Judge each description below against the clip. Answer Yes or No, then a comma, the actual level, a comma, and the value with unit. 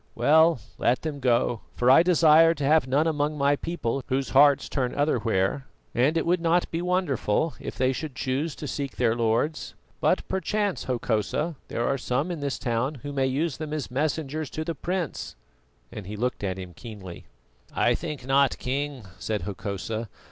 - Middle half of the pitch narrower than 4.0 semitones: No, average, 4.5 semitones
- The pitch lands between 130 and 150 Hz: Yes, medium, 140 Hz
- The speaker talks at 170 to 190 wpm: Yes, average, 180 wpm